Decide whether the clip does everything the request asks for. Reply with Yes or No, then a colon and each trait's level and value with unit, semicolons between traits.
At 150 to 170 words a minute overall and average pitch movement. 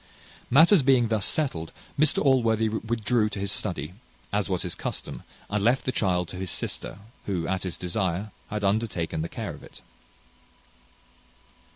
Yes: average, 160 wpm; average, 4.3 semitones